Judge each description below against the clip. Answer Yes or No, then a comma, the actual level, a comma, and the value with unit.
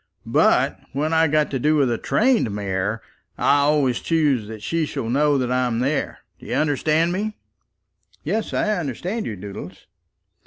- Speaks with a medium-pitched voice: Yes, medium, 145 Hz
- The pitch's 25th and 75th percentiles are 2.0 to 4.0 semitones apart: No, average, 5.2 semitones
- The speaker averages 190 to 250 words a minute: No, average, 165 wpm